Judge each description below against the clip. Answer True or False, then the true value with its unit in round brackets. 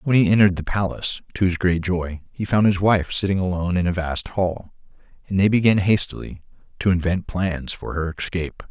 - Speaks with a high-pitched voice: False (90 Hz)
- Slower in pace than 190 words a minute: False (200 wpm)